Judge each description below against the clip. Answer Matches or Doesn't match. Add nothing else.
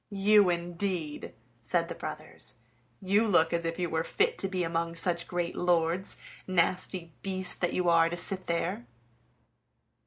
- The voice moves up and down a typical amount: Doesn't match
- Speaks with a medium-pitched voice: Matches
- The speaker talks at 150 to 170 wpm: Matches